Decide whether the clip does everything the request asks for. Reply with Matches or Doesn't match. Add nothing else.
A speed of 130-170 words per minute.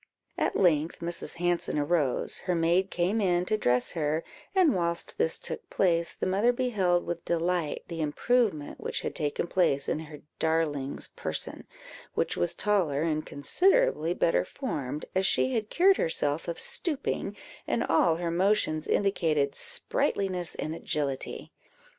Matches